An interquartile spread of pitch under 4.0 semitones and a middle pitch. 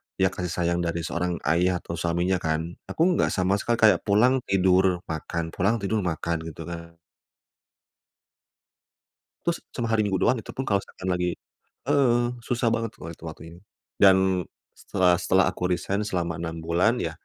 No: average, 3.0 semitones; very low, 90 Hz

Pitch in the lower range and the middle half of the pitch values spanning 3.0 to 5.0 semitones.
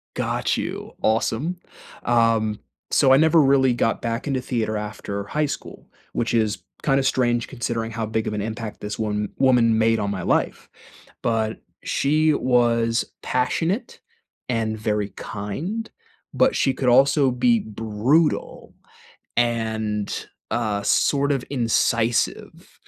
Yes: low, 115 Hz; average, 3.5 semitones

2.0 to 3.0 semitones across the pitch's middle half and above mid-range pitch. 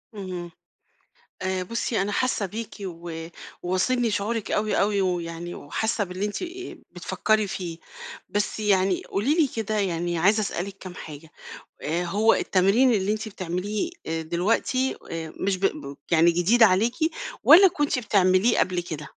No: average, 3.8 semitones; high, 195 Hz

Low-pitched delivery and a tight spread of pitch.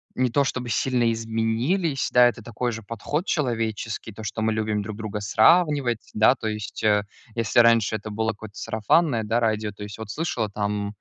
Yes: low, 110 Hz; narrow, 2.3 semitones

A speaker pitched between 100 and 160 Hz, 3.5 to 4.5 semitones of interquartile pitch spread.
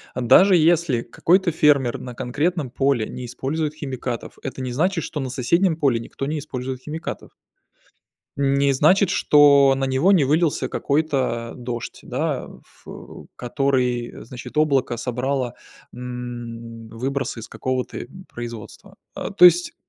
Yes: low, 135 Hz; average, 3.8 semitones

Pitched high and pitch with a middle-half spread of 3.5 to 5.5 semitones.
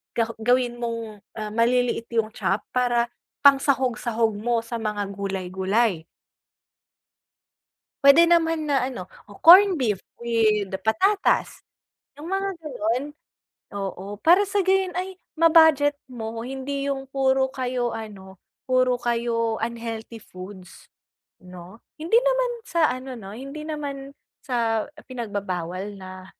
Yes: high, 240 Hz; average, 4.6 semitones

